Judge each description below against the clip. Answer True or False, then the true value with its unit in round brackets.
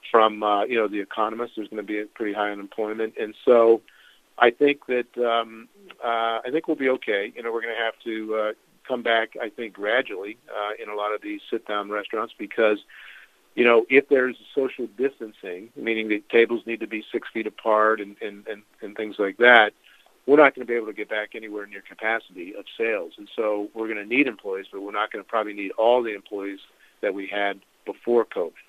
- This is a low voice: True (110 Hz)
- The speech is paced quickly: True (220 wpm)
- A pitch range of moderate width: False (2.1 semitones)